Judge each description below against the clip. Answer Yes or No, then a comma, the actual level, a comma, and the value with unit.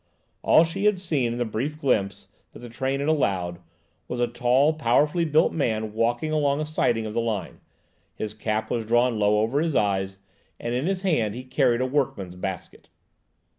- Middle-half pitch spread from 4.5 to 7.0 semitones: Yes, average, 5.3 semitones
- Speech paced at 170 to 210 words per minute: Yes, average, 190 wpm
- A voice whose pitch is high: No, low, 120 Hz